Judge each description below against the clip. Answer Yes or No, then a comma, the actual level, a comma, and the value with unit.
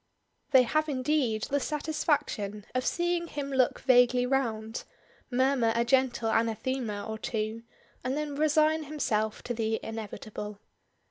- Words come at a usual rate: No, slow, 130 wpm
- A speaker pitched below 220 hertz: No, very high, 250 Hz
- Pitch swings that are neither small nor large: Yes, average, 4.5 semitones